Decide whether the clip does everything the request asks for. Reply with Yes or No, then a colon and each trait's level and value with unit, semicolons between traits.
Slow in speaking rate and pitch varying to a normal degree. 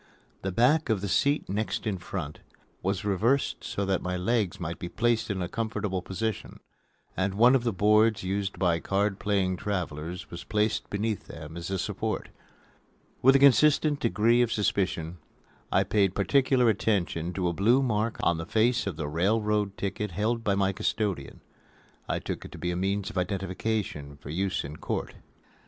No: average, 180 wpm; average, 3.6 semitones